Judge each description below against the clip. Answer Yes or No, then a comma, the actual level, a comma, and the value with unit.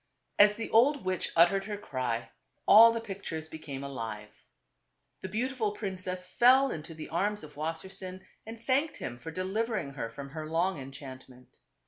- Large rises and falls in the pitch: Yes, wide, 6.9 semitones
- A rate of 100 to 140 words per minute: No, average, 160 wpm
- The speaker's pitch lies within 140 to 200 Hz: Yes, medium, 185 Hz